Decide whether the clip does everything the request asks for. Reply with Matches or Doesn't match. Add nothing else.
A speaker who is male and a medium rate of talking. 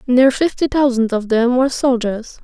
Doesn't match